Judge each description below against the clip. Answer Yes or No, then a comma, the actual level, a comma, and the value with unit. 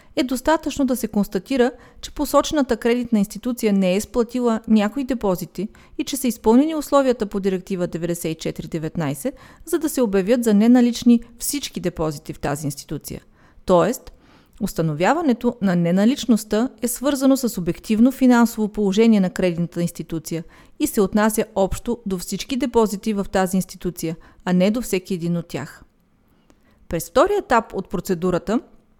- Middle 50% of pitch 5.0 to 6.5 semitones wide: Yes, average, 5.3 semitones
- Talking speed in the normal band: Yes, average, 140 wpm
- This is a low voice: No, high, 215 Hz